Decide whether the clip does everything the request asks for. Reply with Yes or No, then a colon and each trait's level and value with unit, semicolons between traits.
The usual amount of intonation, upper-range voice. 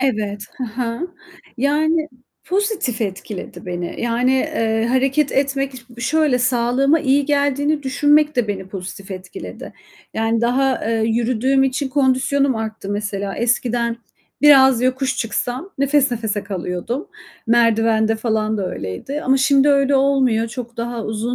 Yes: average, 3.8 semitones; high, 245 Hz